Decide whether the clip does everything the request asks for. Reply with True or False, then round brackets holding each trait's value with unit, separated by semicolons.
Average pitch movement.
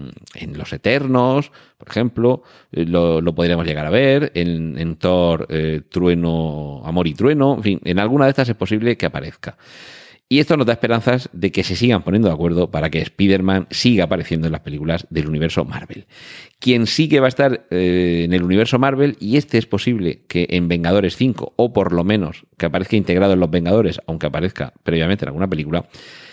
False (6.2 semitones)